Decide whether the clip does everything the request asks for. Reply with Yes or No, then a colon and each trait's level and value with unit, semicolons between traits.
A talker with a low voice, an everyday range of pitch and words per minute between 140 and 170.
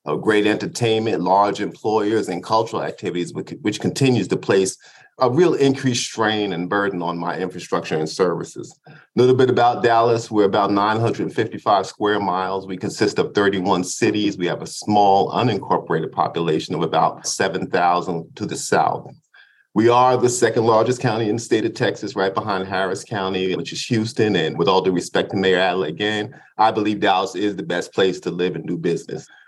No: low, 105 Hz; average, 3.2 semitones; average, 185 wpm